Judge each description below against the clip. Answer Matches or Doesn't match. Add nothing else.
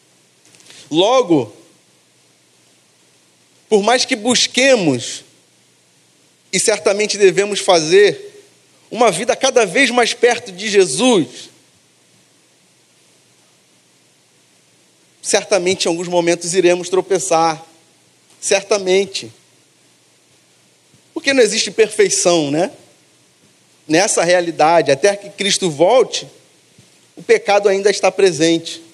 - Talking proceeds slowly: Matches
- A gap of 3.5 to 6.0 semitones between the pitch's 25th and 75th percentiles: Matches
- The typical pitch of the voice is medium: Doesn't match